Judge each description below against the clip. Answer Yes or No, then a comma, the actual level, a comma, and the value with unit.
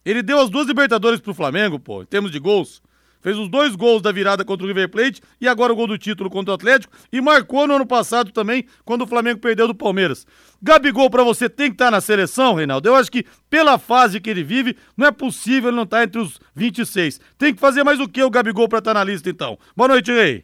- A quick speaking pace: Yes, fast, 260 wpm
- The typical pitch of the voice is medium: No, high, 235 Hz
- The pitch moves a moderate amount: Yes, average, 4.1 semitones